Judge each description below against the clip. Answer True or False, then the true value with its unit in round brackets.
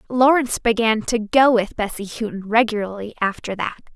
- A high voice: True (225 Hz)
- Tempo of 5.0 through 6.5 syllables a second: True (5.4 syllables/s)